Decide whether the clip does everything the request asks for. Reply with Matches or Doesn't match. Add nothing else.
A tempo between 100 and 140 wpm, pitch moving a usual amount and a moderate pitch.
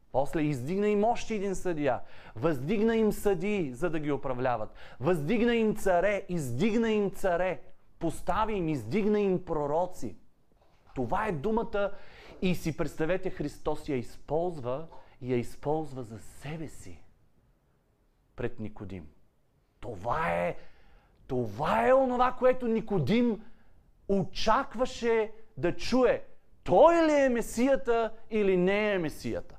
Doesn't match